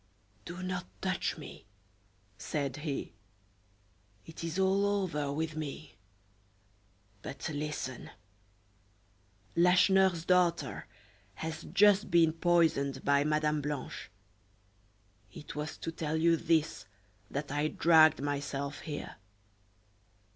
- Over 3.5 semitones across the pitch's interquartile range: No, average, 3.1 semitones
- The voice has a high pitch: No, medium, 155 Hz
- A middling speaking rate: No, slow, 100 wpm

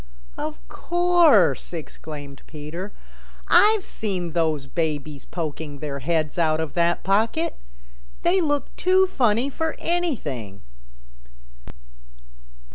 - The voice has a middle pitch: Yes, medium, 170 Hz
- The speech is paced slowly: Yes, slow, 100 wpm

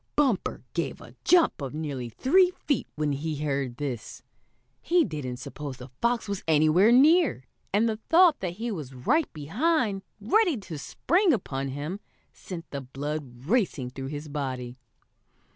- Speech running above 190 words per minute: No, average, 155 wpm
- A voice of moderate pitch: Yes, medium, 160 Hz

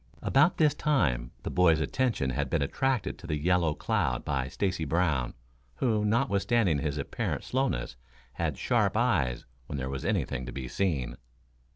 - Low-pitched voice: Yes, very low, 90 Hz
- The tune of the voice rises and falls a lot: Yes, wide, 9.0 semitones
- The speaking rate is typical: Yes, average, 160 wpm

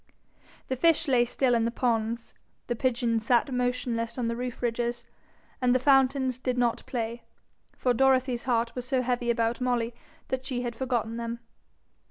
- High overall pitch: Yes, high, 245 Hz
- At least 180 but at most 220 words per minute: No, average, 170 wpm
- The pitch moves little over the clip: Yes, narrow, 1.6 semitones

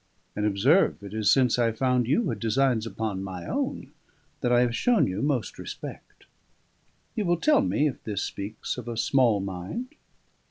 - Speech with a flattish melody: No, average, 4.6 semitones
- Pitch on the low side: Yes, low, 115 Hz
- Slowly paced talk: No, average, 175 wpm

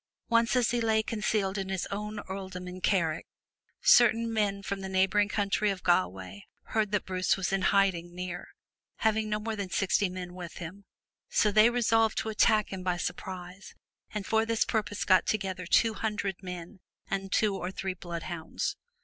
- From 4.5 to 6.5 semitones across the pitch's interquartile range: No, average, 2.8 semitones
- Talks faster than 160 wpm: Yes, average, 175 wpm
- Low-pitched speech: No, high, 195 Hz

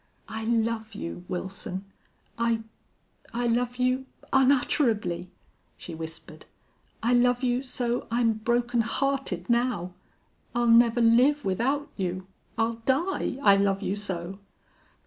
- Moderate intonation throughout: Yes, average, 3.8 semitones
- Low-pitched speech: No, high, 230 Hz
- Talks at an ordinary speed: No, slow, 120 wpm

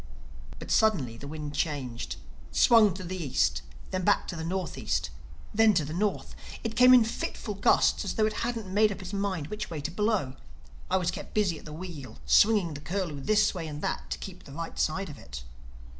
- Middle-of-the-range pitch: Yes, medium, 180 Hz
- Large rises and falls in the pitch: Yes, wide, 5.9 semitones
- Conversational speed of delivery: No, fast, 210 wpm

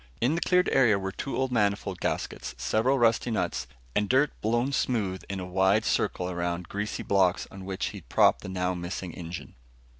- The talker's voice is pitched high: No, low, 100 Hz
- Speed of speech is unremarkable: Yes, average, 185 wpm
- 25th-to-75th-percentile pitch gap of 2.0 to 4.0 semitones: No, average, 4.5 semitones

